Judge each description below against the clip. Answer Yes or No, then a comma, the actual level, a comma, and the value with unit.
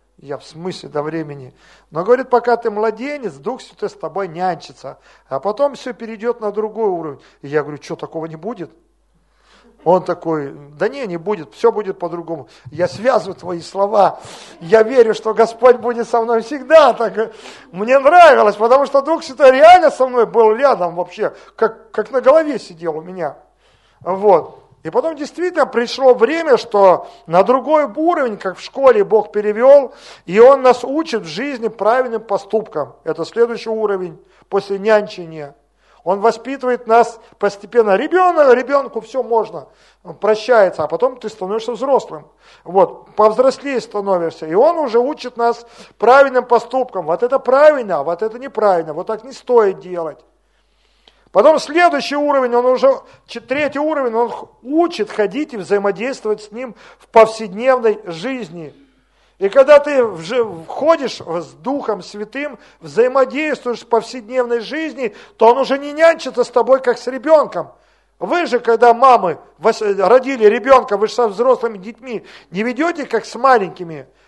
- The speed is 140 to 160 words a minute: Yes, average, 150 wpm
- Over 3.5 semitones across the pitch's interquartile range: Yes, average, 5.1 semitones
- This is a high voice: Yes, high, 230 Hz